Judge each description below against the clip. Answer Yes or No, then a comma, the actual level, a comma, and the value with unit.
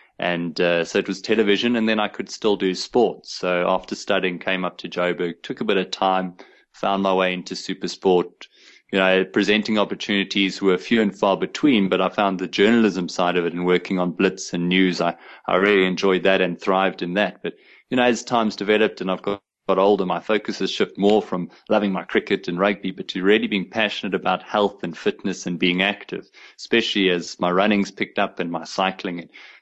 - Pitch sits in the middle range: No, very low, 95 Hz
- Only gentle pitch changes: Yes, narrow, 2.0 semitones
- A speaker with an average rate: No, fast, 215 wpm